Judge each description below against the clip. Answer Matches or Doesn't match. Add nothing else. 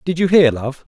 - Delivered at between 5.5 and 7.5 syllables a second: Doesn't match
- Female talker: Doesn't match